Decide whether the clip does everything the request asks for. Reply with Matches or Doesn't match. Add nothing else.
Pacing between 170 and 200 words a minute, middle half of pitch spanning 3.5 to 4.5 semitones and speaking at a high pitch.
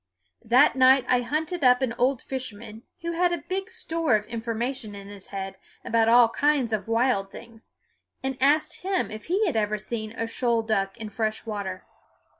Matches